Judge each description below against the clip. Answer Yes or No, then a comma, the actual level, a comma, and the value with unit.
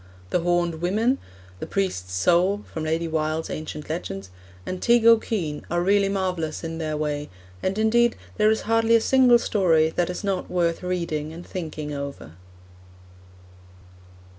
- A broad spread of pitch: No, average, 4.4 semitones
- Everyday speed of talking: No, slow, 130 wpm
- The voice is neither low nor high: Yes, medium, 175 Hz